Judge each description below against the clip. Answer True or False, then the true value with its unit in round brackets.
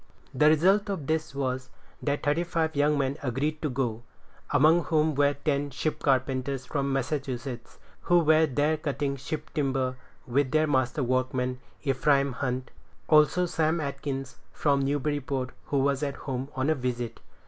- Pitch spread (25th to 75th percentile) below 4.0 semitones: True (2.7 semitones)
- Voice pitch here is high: False (140 Hz)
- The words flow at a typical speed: True (155 wpm)